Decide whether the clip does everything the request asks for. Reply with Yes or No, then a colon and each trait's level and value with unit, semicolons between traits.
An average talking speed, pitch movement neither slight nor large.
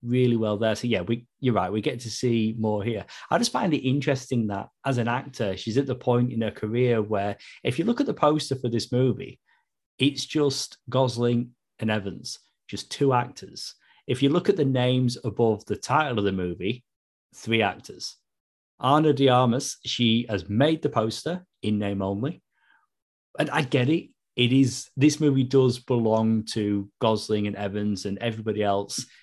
Yes: average, 185 wpm; average, 3.7 semitones